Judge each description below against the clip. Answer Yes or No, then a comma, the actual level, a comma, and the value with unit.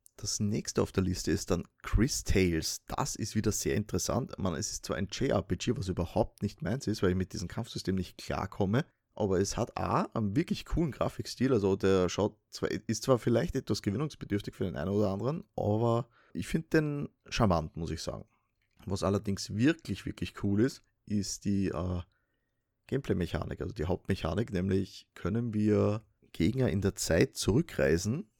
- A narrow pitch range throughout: No, average, 3.2 semitones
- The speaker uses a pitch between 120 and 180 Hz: No, low, 105 Hz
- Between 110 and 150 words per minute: No, average, 175 wpm